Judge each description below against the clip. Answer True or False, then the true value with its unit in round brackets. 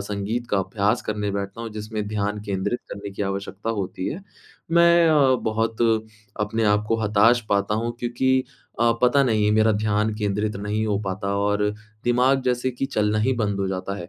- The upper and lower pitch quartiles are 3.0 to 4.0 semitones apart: False (2.6 semitones)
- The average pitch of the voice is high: False (105 Hz)